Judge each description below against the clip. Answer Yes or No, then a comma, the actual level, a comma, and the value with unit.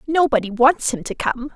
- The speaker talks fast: No, average, 195 wpm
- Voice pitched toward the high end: Yes, very high, 260 Hz